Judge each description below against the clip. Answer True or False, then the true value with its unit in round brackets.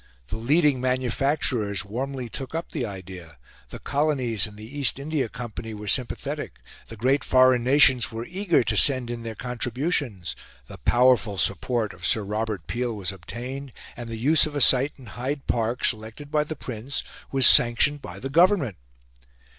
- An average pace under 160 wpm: False (170 wpm)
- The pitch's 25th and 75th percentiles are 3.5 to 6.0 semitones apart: True (4.0 semitones)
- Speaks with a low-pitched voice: True (125 Hz)